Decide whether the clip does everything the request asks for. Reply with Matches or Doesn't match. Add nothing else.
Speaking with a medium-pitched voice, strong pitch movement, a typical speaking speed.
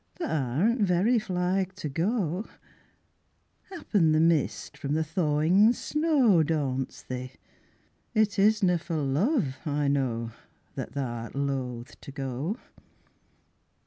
Doesn't match